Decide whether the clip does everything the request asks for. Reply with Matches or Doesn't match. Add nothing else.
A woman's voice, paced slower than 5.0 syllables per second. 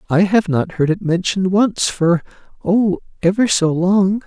Doesn't match